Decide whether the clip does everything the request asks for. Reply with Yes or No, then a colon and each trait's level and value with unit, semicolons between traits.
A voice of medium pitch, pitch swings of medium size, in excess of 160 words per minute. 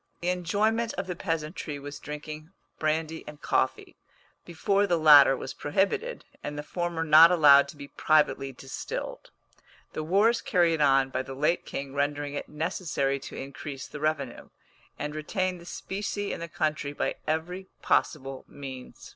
No: medium, 155 Hz; average, 3.6 semitones; average, 155 wpm